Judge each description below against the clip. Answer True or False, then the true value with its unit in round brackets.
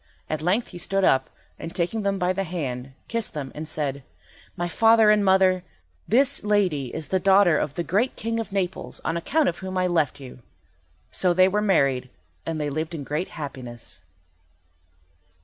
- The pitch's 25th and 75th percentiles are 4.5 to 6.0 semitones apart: True (4.8 semitones)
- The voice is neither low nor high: True (175 Hz)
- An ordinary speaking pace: True (185 wpm)